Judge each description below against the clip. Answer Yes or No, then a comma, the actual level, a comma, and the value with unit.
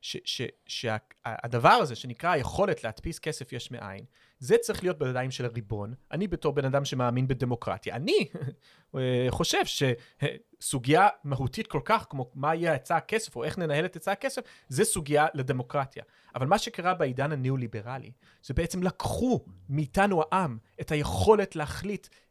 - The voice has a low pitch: No, medium, 145 Hz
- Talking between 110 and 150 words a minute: Yes, average, 145 wpm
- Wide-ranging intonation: Yes, wide, 6.2 semitones